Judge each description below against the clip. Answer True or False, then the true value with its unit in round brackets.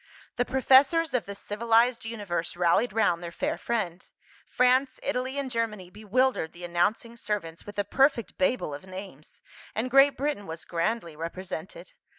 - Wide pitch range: True (6.2 semitones)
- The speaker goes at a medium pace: True (155 wpm)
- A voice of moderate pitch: False (215 Hz)